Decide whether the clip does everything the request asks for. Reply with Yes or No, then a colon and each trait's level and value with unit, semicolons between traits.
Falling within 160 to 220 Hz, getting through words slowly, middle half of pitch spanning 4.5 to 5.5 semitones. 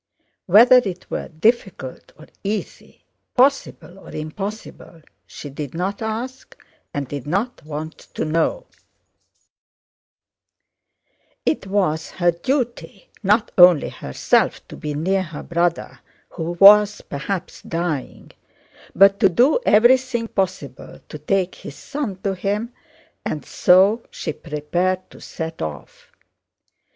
Yes: medium, 185 Hz; slow, 120 wpm; average, 4.8 semitones